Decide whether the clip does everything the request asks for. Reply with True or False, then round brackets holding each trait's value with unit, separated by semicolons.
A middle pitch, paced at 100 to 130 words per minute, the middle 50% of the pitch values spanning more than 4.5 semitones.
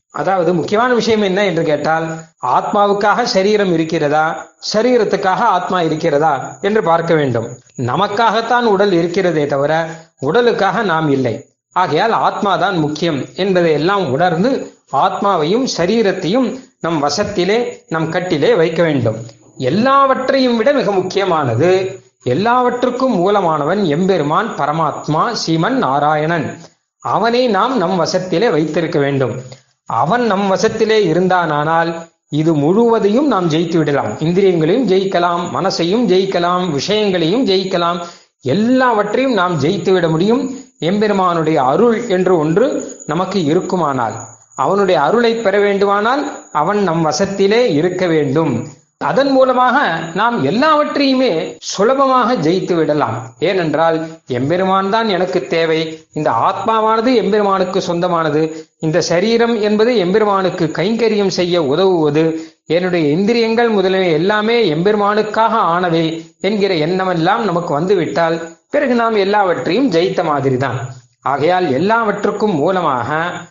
True (180 Hz; 105 wpm; 4.9 semitones)